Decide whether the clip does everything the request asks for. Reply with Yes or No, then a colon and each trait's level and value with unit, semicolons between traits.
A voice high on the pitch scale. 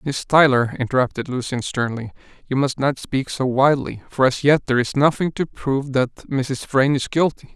No: low, 135 Hz